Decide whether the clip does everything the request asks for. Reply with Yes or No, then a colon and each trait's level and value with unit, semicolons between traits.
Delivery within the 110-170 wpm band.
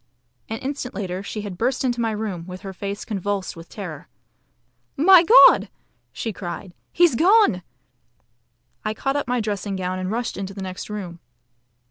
Yes: average, 165 wpm